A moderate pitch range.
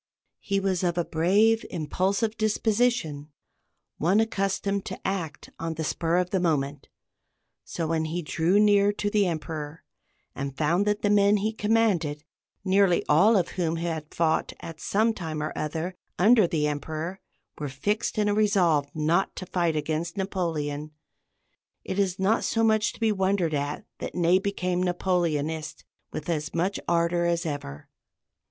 Yes: average, 4.1 semitones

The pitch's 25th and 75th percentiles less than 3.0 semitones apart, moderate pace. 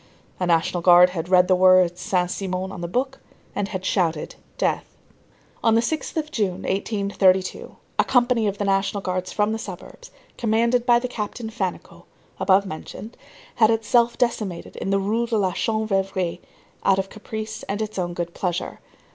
No: average, 3.4 semitones; average, 170 wpm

